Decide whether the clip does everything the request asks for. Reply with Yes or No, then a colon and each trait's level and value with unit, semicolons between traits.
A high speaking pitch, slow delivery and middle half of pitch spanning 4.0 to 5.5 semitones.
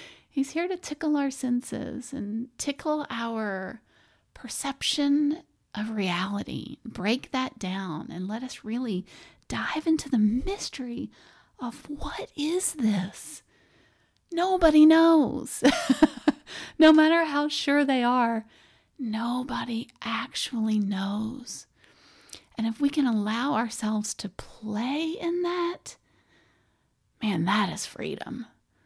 Yes: very high, 255 Hz; slow, 110 wpm; average, 5.2 semitones